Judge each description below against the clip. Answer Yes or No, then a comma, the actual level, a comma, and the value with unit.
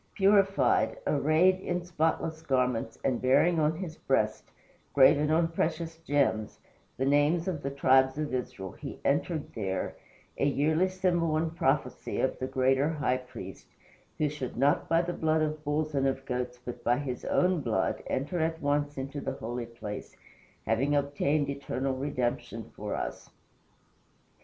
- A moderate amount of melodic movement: Yes, average, 3.6 semitones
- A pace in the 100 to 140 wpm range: No, average, 155 wpm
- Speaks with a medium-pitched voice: Yes, medium, 145 Hz